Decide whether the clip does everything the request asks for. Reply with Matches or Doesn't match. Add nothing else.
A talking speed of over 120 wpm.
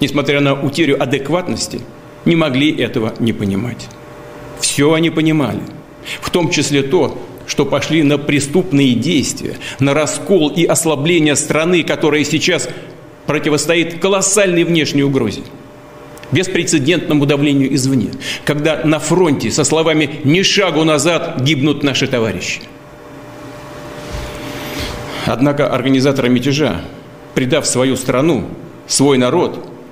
Doesn't match